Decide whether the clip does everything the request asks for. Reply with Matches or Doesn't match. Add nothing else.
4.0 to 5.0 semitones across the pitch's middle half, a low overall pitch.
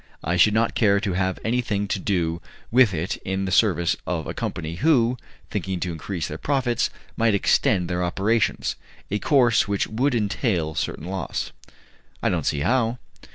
Matches